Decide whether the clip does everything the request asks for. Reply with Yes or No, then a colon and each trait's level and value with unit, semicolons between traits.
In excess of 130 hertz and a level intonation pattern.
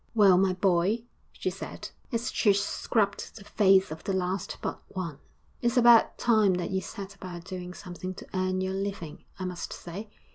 Yes: high, 190 Hz; narrow, 1.9 semitones